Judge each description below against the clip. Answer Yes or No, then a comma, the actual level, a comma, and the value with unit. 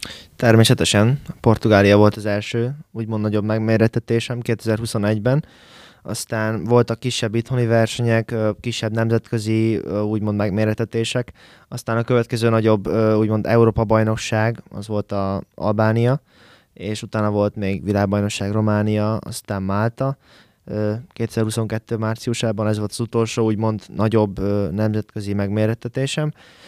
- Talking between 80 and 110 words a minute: Yes, slow, 105 wpm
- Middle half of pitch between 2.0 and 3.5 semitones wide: No, narrow, 1.6 semitones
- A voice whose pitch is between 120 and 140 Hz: No, low, 110 Hz